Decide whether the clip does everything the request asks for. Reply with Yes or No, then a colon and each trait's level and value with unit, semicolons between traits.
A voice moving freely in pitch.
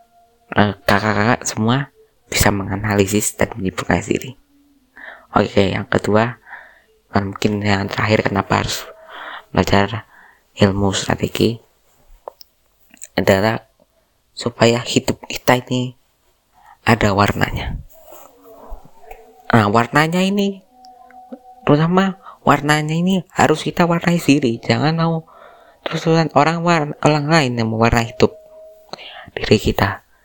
Yes: wide, 8.5 semitones